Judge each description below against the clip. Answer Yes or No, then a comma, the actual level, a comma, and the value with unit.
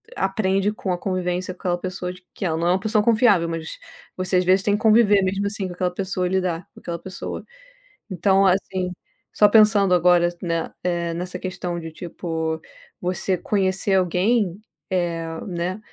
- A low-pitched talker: No, medium, 185 Hz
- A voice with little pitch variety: Yes, narrow, 1.9 semitones